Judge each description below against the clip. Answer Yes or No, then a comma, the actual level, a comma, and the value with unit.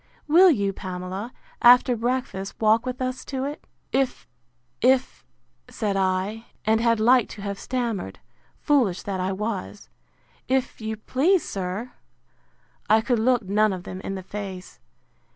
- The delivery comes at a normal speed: Yes, average, 145 wpm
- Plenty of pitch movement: No, average, 4.5 semitones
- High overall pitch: Yes, high, 220 Hz